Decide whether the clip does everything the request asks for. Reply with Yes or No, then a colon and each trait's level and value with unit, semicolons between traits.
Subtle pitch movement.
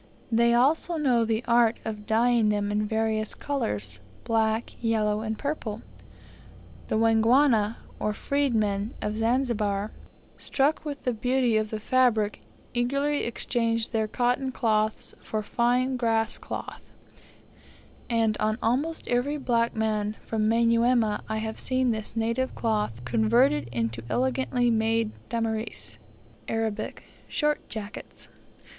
Yes: narrow, 2.2 semitones